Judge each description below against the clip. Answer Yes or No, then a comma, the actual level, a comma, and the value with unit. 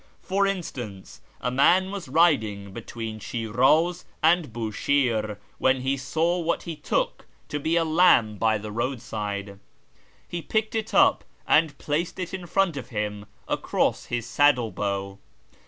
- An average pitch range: No, wide, 7.7 semitones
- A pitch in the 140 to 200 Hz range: No, low, 130 Hz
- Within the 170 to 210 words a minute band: No, average, 145 wpm